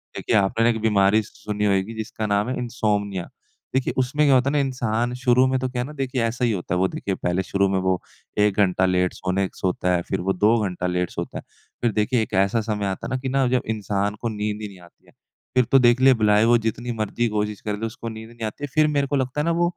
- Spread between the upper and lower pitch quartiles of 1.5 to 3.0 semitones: No, average, 4.1 semitones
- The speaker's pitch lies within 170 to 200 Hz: No, low, 110 Hz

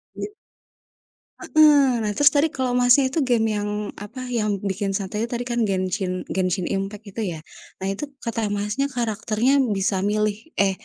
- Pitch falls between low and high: No, high, 215 Hz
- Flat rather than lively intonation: No, average, 3.9 semitones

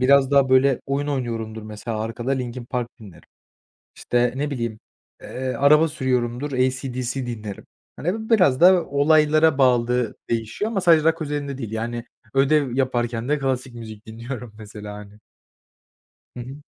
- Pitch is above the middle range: No, low, 130 Hz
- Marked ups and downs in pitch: No, average, 3.3 semitones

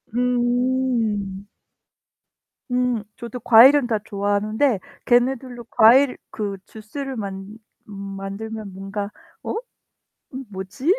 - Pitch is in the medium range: No, high, 220 Hz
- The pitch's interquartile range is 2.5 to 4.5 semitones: Yes, average, 3.7 semitones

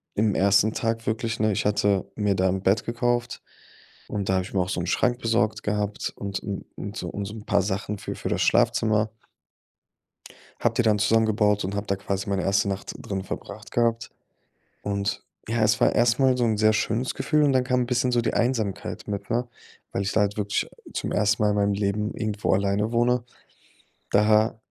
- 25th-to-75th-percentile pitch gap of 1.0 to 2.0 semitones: No, narrow, 2.4 semitones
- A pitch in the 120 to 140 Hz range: No, low, 105 Hz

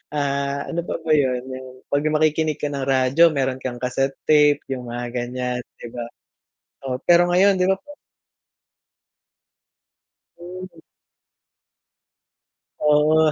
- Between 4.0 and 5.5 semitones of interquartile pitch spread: No, average, 3.4 semitones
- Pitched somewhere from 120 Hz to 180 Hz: Yes, medium, 140 Hz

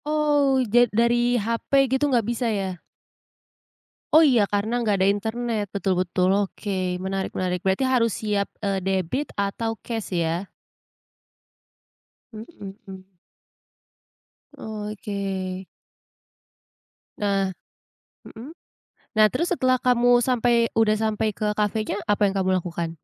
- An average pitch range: Yes, average, 3.7 semitones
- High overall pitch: Yes, high, 210 Hz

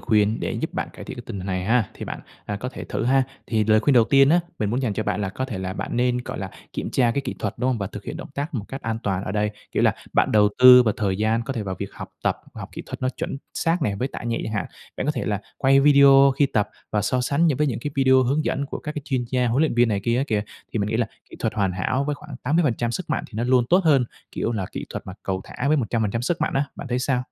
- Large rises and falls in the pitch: No, average, 4.4 semitones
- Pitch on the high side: No, low, 120 Hz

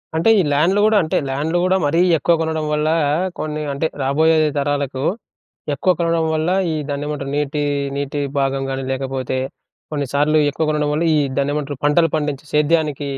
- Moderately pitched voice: Yes, medium, 150 Hz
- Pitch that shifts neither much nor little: No, narrow, 2.1 semitones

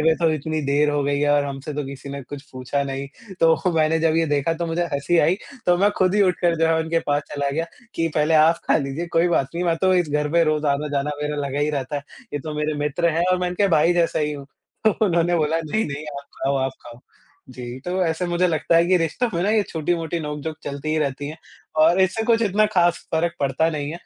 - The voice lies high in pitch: No, medium, 155 Hz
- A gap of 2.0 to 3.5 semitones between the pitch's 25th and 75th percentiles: Yes, average, 3.0 semitones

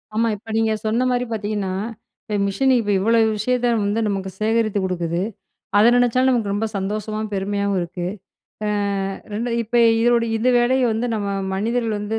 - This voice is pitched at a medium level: No, high, 215 Hz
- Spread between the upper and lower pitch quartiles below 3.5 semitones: Yes, narrow, 2.5 semitones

